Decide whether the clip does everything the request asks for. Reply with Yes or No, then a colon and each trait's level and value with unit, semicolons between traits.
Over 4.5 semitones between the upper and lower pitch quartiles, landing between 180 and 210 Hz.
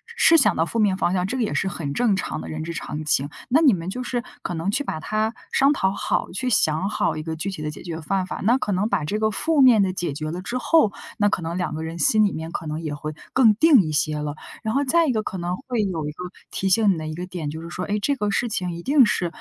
Yes: wide, 5.6 semitones; high, 190 Hz